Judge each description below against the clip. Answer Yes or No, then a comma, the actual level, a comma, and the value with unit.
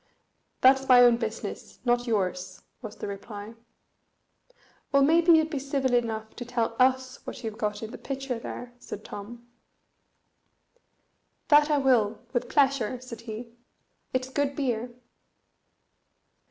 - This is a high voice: Yes, high, 245 Hz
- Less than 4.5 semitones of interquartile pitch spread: Yes, average, 3.4 semitones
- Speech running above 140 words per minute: No, slow, 135 wpm